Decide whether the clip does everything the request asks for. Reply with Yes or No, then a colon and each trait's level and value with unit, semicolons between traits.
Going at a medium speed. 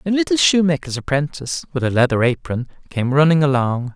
Yes: average, 165 wpm